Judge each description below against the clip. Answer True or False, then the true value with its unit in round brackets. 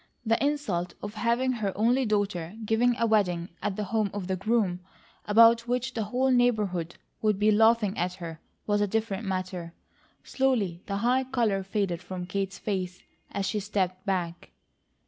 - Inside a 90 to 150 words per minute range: False (165 wpm)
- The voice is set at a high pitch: True (205 Hz)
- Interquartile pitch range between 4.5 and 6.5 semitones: False (3.8 semitones)